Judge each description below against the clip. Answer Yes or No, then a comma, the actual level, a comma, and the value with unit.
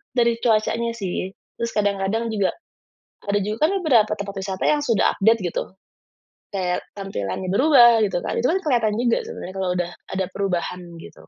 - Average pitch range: Yes, average, 3.5 semitones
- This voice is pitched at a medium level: No, high, 210 Hz